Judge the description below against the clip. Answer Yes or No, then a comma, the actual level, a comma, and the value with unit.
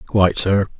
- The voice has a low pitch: Yes, low, 100 Hz